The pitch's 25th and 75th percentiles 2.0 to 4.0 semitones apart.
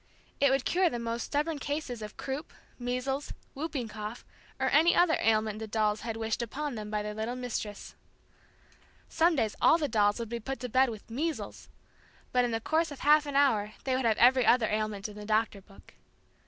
No: average, 4.7 semitones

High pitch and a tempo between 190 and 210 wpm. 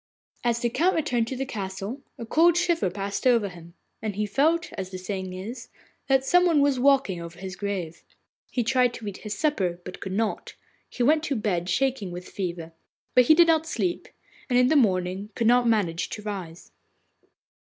Yes: high, 220 Hz; average, 195 wpm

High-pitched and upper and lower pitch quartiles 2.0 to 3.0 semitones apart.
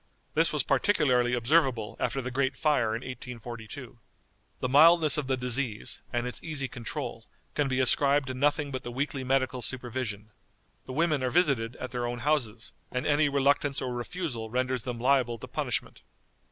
No: low, 130 Hz; average, 2.7 semitones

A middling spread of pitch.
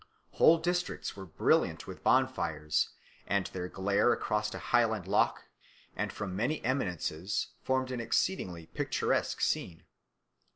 No: wide, 6.1 semitones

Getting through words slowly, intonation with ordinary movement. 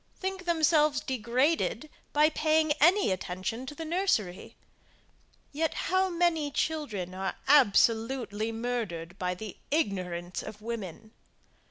No: slow, 115 wpm; wide, 7.7 semitones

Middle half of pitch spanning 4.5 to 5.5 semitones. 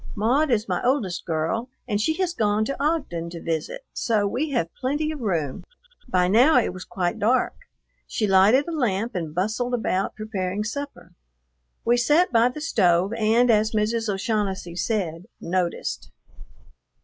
Yes: average, 5.2 semitones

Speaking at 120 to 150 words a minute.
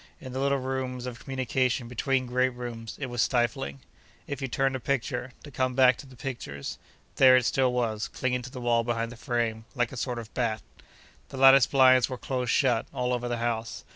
No: average, 200 wpm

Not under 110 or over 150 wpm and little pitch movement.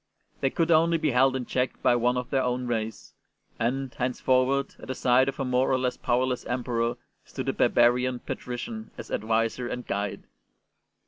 No: average, 190 wpm; narrow, 1.6 semitones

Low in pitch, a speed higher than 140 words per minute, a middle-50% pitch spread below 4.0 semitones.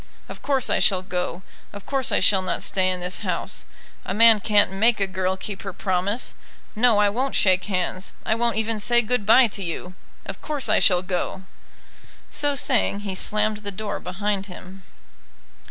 No: high, 205 Hz; average, 185 wpm; average, 3.1 semitones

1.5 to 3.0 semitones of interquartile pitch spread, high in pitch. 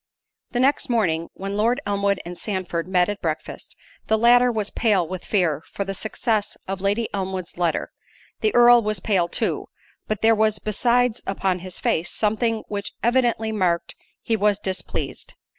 No: average, 3.4 semitones; high, 205 Hz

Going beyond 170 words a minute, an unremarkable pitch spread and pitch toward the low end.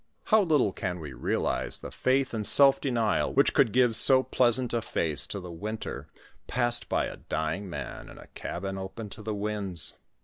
Yes: average, 190 wpm; average, 5.0 semitones; low, 110 Hz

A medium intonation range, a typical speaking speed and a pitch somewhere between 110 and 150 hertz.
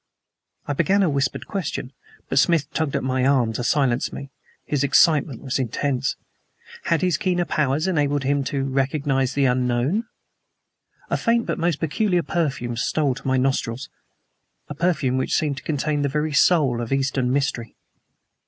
Yes: average, 3.0 semitones; average, 160 wpm; medium, 140 Hz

